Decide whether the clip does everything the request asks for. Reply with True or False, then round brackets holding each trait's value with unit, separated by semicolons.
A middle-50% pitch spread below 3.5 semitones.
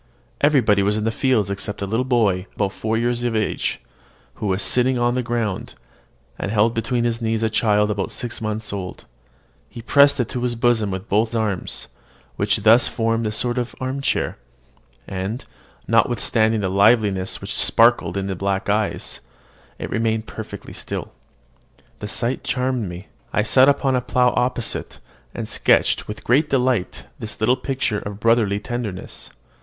True (2.9 semitones)